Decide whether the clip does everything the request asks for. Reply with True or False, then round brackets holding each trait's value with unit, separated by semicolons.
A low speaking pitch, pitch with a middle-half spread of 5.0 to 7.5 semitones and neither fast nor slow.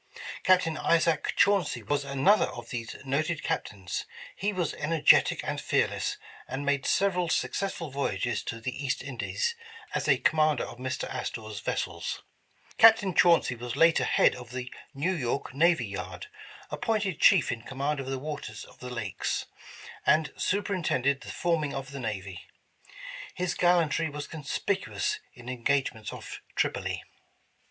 False (145 Hz; 5.3 semitones; 150 wpm)